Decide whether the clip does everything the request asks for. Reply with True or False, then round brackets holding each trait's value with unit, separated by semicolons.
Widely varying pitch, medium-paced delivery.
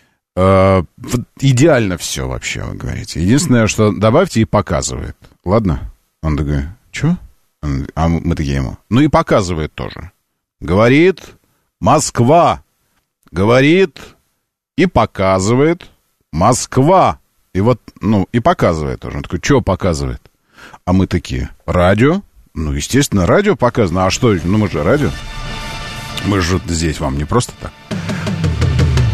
True (7.2 semitones; 125 wpm)